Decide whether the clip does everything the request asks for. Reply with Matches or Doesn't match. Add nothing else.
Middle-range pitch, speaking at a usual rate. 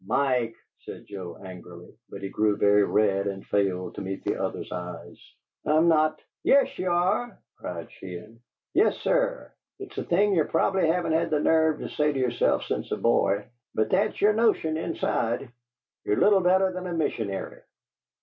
Matches